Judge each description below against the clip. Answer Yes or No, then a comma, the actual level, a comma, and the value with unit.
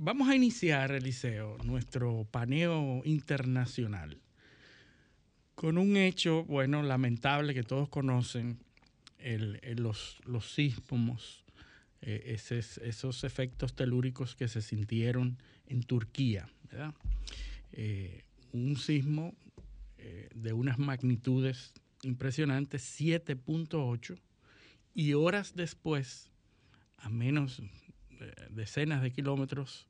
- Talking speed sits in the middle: No, slow, 100 wpm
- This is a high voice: No, low, 130 Hz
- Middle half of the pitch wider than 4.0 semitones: No, average, 3.4 semitones